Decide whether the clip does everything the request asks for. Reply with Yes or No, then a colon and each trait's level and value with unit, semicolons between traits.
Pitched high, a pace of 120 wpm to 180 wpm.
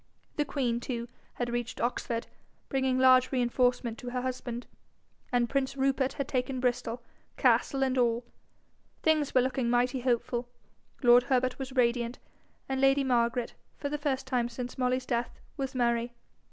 Yes: very high, 250 Hz; average, 155 wpm